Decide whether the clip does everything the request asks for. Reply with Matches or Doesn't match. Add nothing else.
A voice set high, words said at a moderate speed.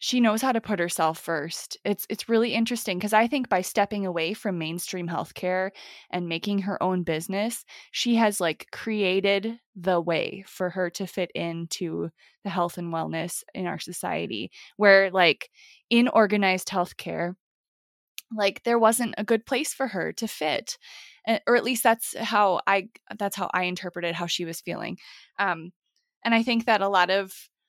Matches